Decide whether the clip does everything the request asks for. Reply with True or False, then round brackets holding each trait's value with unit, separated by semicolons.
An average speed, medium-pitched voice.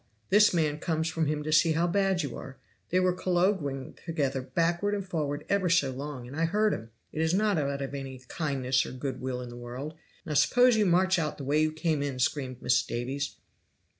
False (220 wpm; 155 Hz)